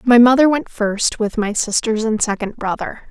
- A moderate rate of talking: Yes, average, 195 wpm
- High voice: Yes, high, 225 Hz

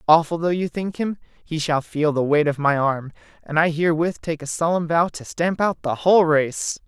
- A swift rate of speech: Yes, fast, 225 wpm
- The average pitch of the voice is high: No, medium, 160 Hz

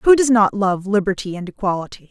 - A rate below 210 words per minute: Yes, average, 200 wpm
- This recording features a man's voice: No, female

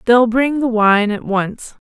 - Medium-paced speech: Yes, average, 195 wpm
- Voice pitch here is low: No, high, 230 Hz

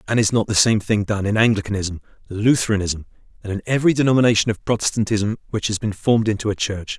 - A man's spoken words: Yes, male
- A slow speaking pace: No, average, 190 wpm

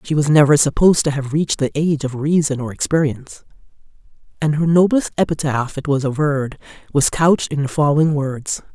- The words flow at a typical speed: Yes, average, 180 wpm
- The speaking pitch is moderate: Yes, medium, 145 Hz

